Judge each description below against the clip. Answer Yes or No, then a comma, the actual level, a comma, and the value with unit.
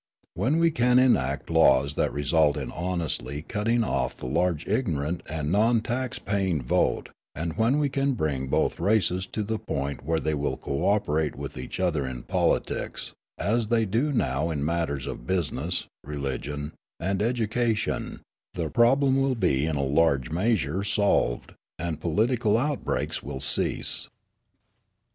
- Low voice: Yes, very low, 85 Hz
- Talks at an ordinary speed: Yes, average, 155 wpm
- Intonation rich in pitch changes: Yes, wide, 7.5 semitones